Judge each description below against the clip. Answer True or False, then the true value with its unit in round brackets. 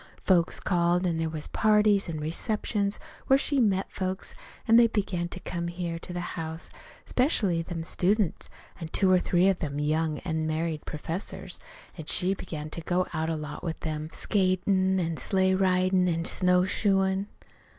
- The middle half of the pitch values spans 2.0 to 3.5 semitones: True (2.8 semitones)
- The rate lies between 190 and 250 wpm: False (165 wpm)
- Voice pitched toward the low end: False (180 Hz)